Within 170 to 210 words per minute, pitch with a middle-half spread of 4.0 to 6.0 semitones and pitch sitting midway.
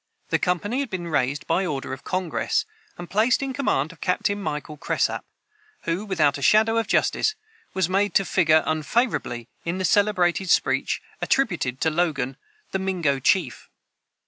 No: average, 160 wpm; average, 4.9 semitones; medium, 180 Hz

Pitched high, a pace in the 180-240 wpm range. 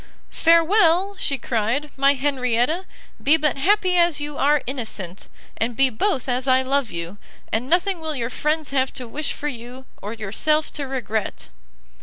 No: very high, 275 Hz; average, 165 wpm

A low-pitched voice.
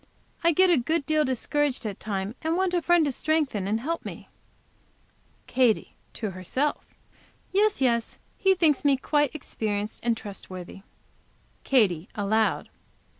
No: very high, 260 Hz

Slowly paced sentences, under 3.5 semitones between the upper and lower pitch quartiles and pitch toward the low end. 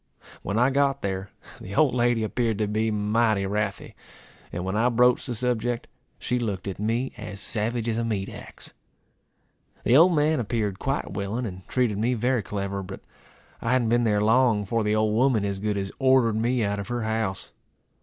No: average, 195 wpm; average, 3.1 semitones; low, 110 Hz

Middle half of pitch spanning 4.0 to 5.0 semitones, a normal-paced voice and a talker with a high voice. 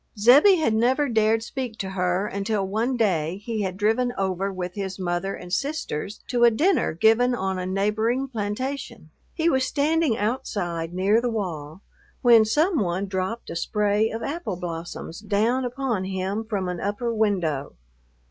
Yes: average, 4.5 semitones; average, 165 wpm; high, 210 Hz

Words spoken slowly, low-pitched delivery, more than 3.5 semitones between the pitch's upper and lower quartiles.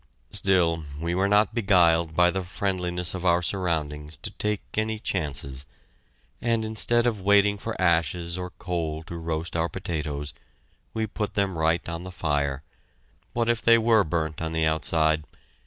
No: average, 160 wpm; very low, 85 Hz; average, 4.0 semitones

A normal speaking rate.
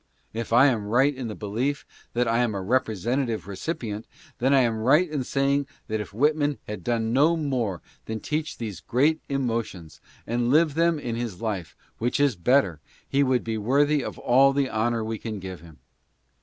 No: fast, 210 wpm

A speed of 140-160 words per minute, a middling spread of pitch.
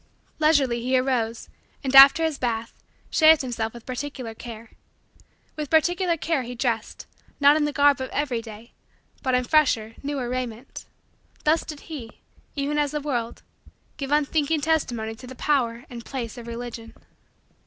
Yes: average, 155 wpm; average, 4.0 semitones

